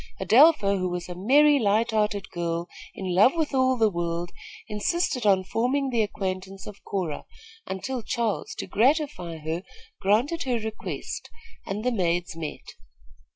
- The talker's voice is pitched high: Yes, high, 205 Hz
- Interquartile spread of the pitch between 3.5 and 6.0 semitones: Yes, wide, 5.6 semitones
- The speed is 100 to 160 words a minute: Yes, average, 150 wpm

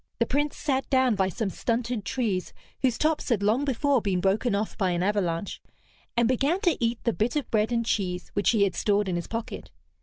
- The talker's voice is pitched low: No, high, 225 Hz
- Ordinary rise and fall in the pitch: Yes, average, 4.2 semitones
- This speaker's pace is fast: Yes, fast, 215 wpm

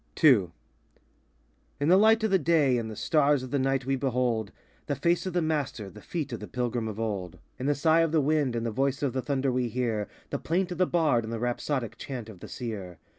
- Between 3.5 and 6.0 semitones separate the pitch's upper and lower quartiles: Yes, average, 5.0 semitones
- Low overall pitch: Yes, low, 130 Hz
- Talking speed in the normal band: No, fast, 245 wpm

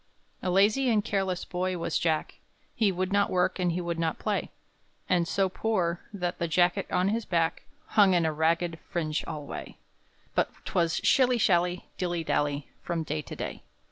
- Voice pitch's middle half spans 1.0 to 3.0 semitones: Yes, narrow, 2.6 semitones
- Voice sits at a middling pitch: Yes, medium, 175 Hz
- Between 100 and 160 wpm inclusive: No, average, 175 wpm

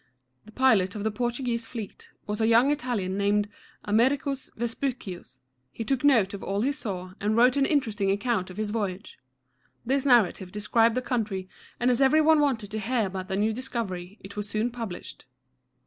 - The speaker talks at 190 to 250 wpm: Yes, average, 195 wpm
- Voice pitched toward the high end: Yes, high, 220 Hz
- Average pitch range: Yes, average, 3.9 semitones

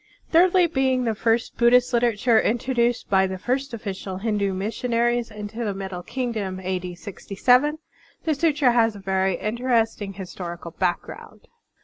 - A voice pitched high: Yes, high, 225 Hz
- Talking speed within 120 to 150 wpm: Yes, average, 140 wpm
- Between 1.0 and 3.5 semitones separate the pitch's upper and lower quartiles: No, average, 4.3 semitones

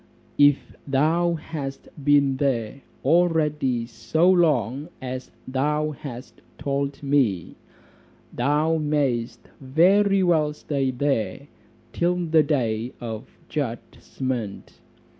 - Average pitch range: Yes, average, 3.5 semitones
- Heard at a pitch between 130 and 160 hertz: Yes, medium, 140 Hz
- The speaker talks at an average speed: No, slow, 95 wpm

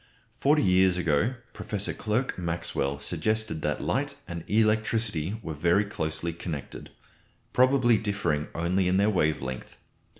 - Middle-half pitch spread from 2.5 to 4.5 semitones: No, average, 5.1 semitones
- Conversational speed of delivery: No, slow, 130 wpm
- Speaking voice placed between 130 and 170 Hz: No, very low, 90 Hz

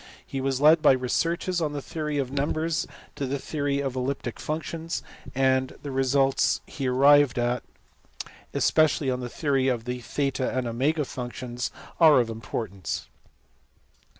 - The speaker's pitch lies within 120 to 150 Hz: Yes, low, 135 Hz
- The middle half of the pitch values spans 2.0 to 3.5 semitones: Yes, average, 2.7 semitones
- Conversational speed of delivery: Yes, average, 150 wpm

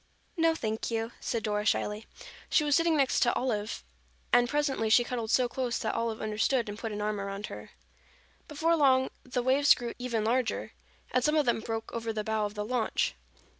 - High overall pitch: Yes, high, 235 Hz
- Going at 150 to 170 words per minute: No, average, 195 wpm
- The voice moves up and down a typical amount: Yes, average, 3.2 semitones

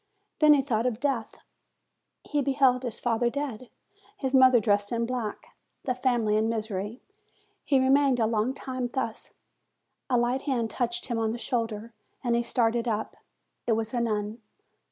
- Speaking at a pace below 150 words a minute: No, average, 165 wpm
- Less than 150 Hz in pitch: No, high, 240 Hz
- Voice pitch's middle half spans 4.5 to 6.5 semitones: No, narrow, 2.6 semitones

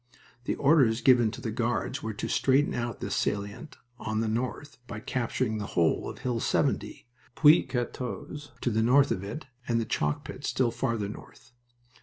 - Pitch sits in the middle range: No, low, 120 Hz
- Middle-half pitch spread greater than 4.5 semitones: No, average, 2.9 semitones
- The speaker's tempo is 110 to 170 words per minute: No, average, 180 wpm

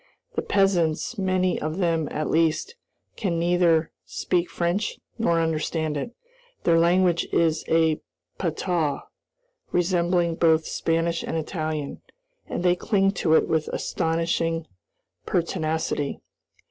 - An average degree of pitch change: No, narrow, 1.9 semitones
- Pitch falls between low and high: Yes, medium, 165 Hz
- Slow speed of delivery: Yes, slow, 115 wpm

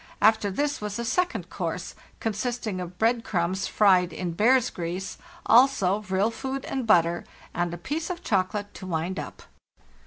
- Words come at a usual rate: Yes, average, 160 wpm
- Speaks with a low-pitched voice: No, high, 205 Hz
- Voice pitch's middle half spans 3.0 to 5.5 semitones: Yes, average, 4.7 semitones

